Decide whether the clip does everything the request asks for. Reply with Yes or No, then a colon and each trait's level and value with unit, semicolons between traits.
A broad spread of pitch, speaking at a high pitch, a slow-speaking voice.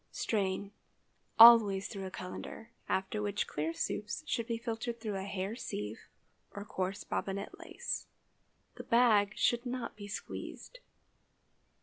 No: average, 3.2 semitones; high, 205 Hz; slow, 125 wpm